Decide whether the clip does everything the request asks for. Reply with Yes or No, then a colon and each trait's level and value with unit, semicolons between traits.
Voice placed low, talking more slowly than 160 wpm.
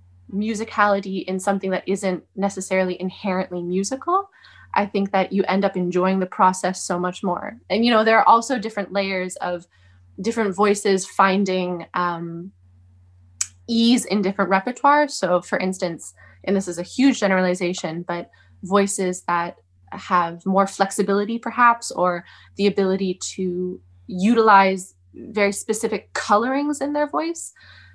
No: high, 190 Hz; slow, 135 wpm